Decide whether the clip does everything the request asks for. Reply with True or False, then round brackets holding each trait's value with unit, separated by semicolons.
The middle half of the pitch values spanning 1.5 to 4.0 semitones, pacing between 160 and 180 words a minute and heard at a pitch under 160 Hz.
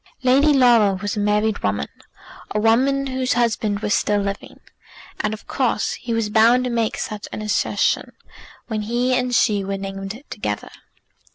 False (3.2 semitones; 165 wpm; 220 Hz)